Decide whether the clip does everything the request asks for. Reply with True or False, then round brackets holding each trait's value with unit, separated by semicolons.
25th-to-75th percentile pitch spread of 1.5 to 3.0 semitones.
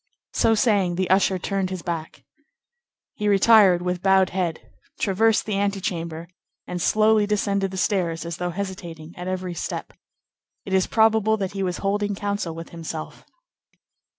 True (2.6 semitones)